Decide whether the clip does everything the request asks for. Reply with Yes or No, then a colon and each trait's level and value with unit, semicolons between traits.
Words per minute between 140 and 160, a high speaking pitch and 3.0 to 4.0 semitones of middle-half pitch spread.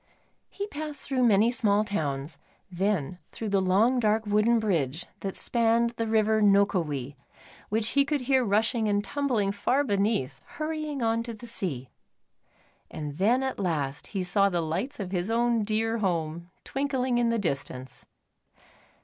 No: average, 155 wpm; high, 215 Hz; average, 4.6 semitones